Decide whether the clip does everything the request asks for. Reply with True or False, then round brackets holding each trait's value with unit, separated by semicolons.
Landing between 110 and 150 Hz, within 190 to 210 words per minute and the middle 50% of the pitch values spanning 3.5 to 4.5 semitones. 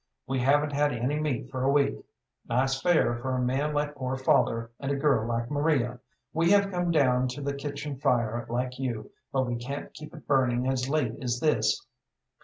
False (135 Hz; 200 wpm; 2.9 semitones)